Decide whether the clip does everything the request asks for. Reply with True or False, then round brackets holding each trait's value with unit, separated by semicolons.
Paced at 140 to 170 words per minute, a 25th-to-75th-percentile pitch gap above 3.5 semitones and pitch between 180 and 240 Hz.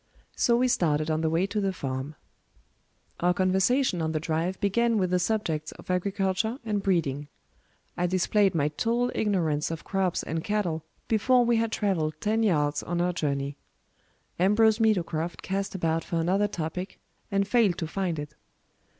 True (165 wpm; 4.5 semitones; 185 Hz)